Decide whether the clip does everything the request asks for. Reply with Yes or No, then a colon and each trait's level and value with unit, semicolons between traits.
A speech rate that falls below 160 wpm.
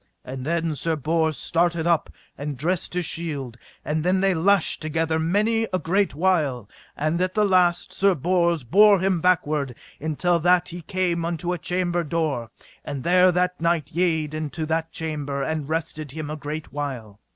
No: average, 175 wpm